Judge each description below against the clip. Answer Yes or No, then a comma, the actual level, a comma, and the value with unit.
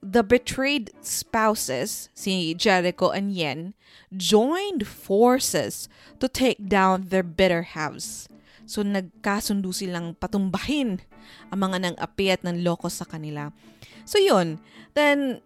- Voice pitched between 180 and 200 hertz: Yes, high, 190 Hz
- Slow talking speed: Yes, slow, 115 wpm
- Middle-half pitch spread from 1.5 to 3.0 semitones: No, average, 3.8 semitones